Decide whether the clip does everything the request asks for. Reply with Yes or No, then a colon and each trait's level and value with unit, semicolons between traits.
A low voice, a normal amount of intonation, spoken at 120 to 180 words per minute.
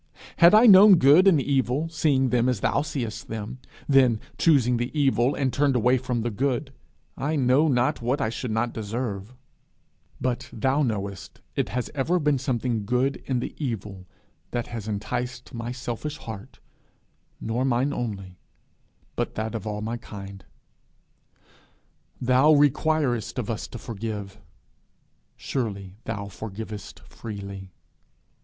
Yes: low, 120 Hz; average, 3.8 semitones; average, 140 wpm